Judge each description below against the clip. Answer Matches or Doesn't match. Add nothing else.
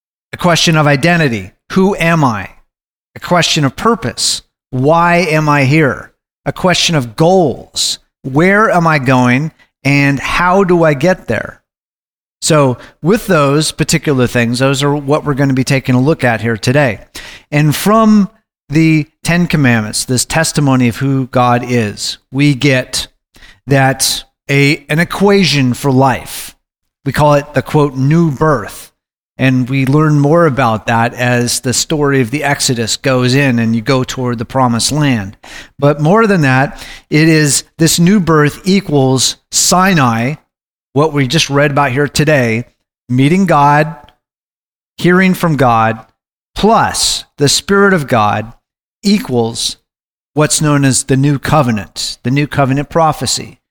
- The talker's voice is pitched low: Doesn't match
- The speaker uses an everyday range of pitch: Matches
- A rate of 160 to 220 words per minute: Doesn't match